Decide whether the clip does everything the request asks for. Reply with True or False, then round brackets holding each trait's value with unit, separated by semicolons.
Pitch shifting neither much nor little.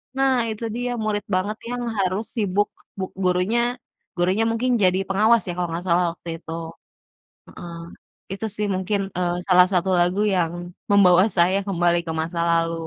True (3.1 semitones)